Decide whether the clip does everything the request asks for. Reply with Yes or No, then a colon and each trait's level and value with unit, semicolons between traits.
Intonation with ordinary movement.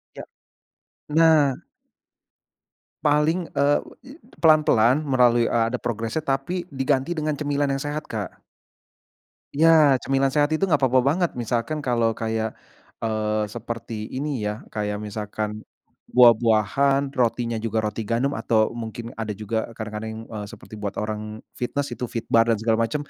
Yes: average, 4.5 semitones